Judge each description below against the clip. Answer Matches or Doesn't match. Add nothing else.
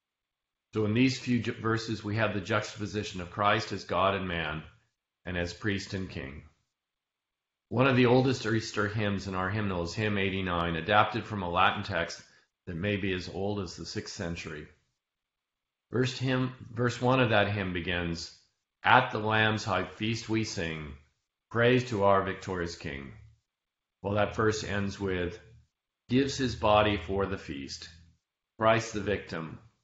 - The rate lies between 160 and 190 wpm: Matches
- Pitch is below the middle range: Matches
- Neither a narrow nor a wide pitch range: Matches